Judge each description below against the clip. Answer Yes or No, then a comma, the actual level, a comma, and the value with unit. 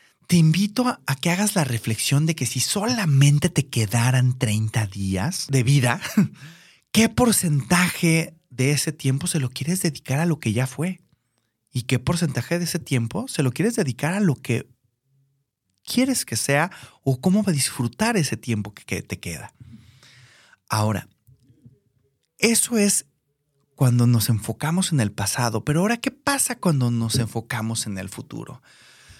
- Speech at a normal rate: Yes, average, 155 wpm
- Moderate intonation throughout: No, wide, 6.3 semitones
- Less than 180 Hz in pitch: Yes, low, 135 Hz